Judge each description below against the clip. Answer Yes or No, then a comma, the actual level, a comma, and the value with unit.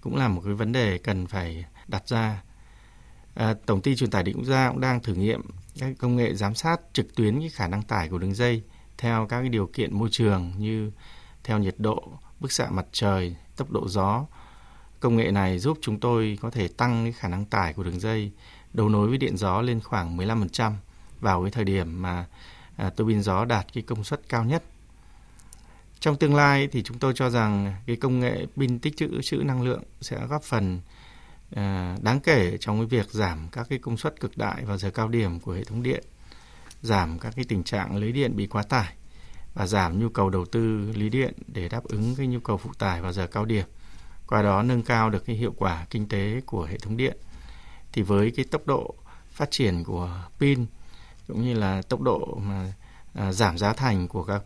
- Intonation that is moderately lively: Yes, average, 4.0 semitones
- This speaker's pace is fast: No, average, 215 wpm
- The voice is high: No, low, 110 Hz